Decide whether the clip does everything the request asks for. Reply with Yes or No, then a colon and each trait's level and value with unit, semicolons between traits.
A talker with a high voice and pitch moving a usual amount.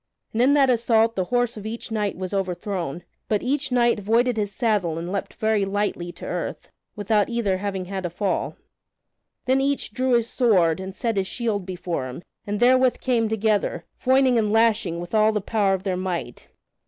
Yes: high, 210 Hz; average, 3.9 semitones